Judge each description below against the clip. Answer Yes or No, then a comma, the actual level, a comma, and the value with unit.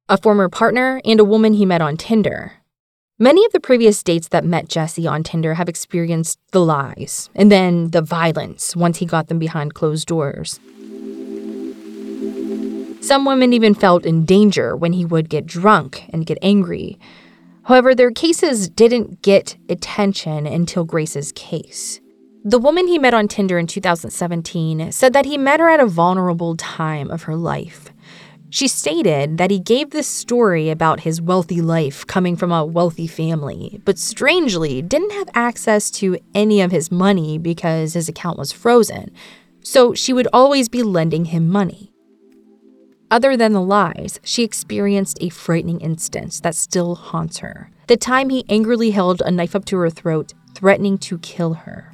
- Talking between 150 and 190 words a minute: Yes, average, 170 wpm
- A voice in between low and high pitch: Yes, medium, 180 Hz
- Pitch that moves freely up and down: No, average, 4.7 semitones